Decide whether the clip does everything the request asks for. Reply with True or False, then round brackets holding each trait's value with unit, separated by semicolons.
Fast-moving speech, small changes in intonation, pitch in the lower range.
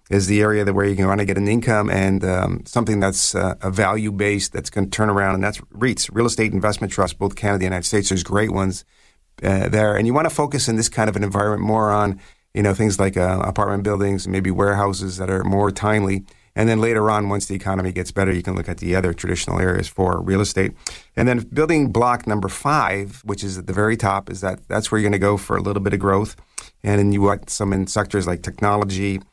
True (255 wpm; 1.7 semitones; 100 Hz)